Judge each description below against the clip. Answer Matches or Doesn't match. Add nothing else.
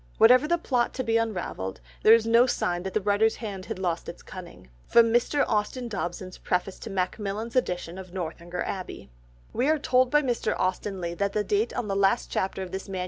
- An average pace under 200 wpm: Doesn't match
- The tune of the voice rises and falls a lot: Doesn't match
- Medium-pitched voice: Doesn't match